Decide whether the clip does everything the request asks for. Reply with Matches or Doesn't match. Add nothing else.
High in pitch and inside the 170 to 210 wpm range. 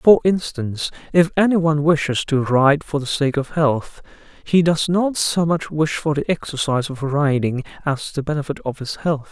Doesn't match